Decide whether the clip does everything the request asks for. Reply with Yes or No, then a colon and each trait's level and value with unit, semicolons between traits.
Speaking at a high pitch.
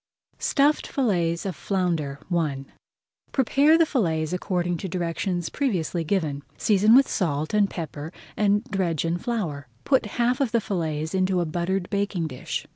No: medium, 180 Hz